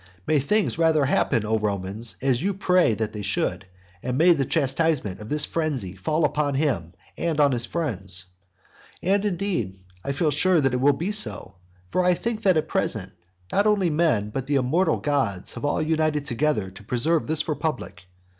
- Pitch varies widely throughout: Yes, wide, 6.6 semitones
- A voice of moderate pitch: Yes, medium, 145 Hz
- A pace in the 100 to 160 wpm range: No, average, 185 wpm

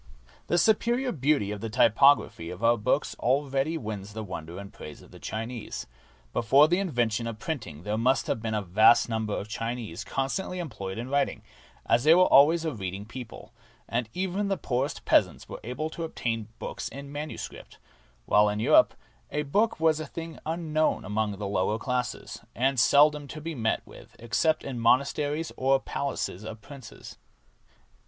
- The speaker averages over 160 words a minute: Yes, average, 175 wpm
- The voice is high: No, low, 125 Hz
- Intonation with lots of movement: Yes, wide, 5.8 semitones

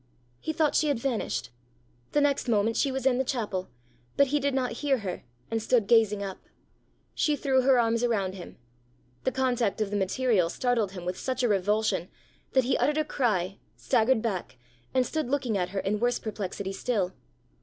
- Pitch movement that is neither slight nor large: Yes, average, 4.8 semitones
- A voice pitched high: Yes, high, 230 Hz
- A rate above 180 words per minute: Yes, average, 190 wpm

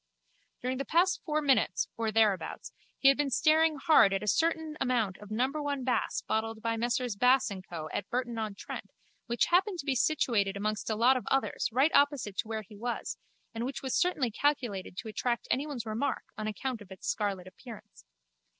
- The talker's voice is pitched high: Yes, high, 240 Hz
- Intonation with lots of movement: No, average, 4.5 semitones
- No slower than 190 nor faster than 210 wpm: Yes, average, 195 wpm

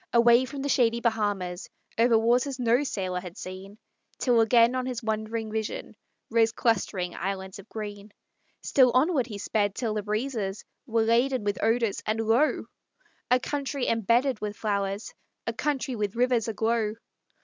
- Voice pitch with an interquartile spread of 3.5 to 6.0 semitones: No, average, 3.0 semitones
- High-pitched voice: Yes, high, 225 Hz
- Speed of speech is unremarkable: Yes, average, 155 wpm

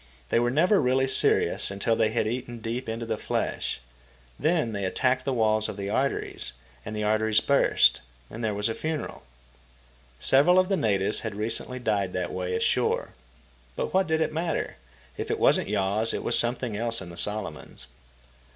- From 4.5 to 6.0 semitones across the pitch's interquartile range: No, average, 3.9 semitones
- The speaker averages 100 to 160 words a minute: No, average, 180 wpm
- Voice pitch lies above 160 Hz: No, low, 115 Hz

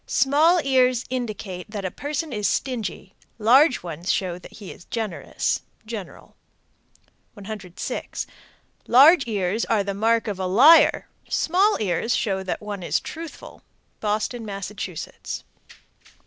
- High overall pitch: Yes, high, 215 Hz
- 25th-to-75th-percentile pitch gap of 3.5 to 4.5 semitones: No, average, 4.9 semitones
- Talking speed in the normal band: No, slow, 130 wpm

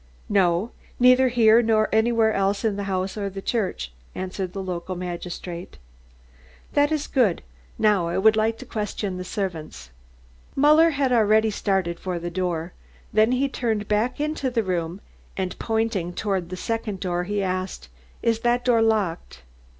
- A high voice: Yes, high, 205 Hz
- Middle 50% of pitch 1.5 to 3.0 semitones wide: No, average, 3.8 semitones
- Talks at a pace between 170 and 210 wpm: No, average, 160 wpm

